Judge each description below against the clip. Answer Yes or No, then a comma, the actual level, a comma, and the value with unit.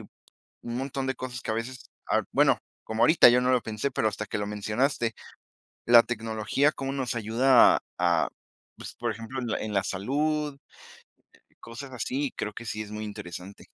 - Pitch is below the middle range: Yes, low, 115 Hz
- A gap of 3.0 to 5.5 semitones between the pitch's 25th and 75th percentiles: Yes, average, 3.7 semitones